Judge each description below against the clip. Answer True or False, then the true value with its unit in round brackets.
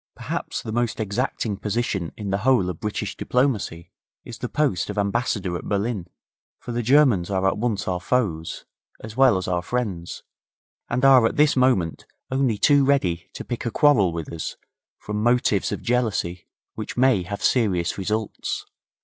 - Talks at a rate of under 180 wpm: True (170 wpm)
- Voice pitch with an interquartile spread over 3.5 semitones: True (4.9 semitones)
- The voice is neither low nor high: False (105 Hz)